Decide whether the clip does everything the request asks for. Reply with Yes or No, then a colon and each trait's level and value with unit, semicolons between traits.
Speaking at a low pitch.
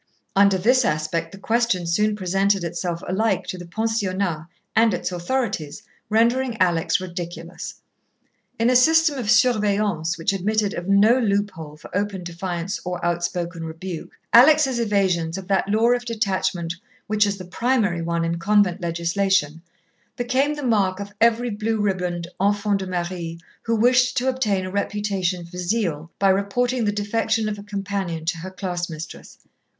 No: high, 195 Hz